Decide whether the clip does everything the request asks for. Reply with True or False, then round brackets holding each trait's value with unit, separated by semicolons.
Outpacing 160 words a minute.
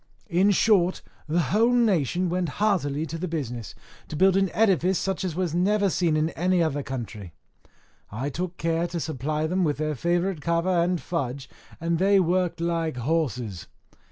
True (170 wpm)